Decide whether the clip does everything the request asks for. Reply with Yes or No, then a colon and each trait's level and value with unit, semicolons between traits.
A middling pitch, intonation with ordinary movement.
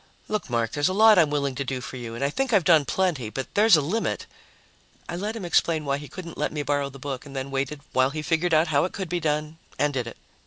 Yes: medium, 150 Hz; average, 4.4 semitones